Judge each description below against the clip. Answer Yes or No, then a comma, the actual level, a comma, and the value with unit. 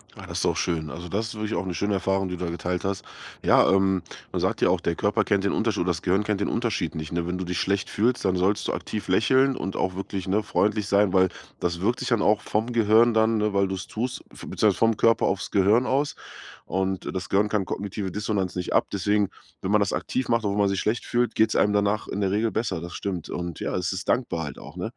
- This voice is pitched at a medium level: No, low, 100 Hz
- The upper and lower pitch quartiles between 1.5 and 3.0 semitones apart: Yes, average, 2.7 semitones